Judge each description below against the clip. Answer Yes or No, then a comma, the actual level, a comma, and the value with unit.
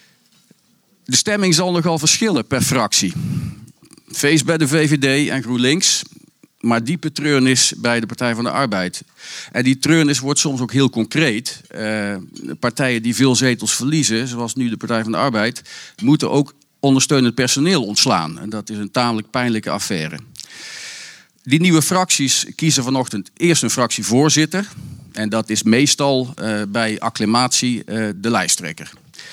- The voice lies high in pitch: No, low, 130 Hz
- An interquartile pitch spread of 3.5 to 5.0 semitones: Yes, average, 4.5 semitones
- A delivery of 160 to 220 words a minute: No, average, 150 wpm